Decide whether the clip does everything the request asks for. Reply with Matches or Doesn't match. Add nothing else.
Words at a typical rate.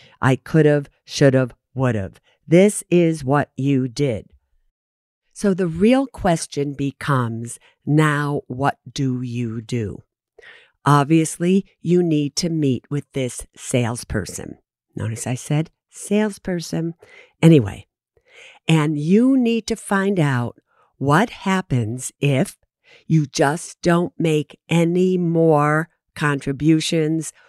Doesn't match